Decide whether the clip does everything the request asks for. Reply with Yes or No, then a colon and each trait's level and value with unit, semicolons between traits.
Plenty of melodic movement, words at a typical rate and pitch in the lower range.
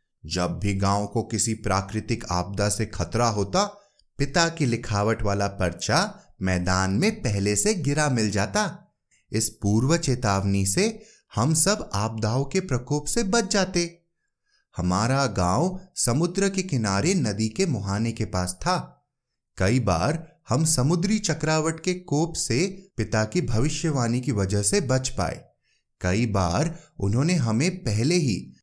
Yes: wide, 8.9 semitones; average, 140 wpm; low, 125 Hz